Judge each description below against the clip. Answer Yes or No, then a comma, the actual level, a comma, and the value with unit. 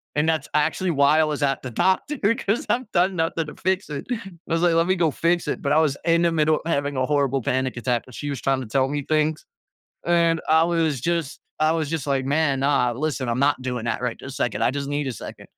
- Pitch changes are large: No, average, 3.5 semitones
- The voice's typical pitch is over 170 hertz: No, medium, 150 Hz